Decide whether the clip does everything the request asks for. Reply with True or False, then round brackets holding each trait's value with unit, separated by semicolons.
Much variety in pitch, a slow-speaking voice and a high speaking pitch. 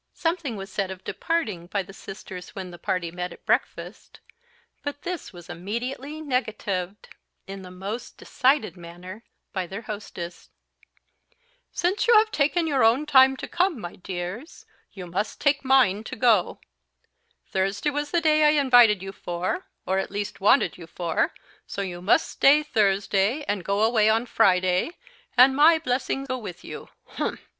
False (6.9 semitones; 165 wpm; 215 Hz)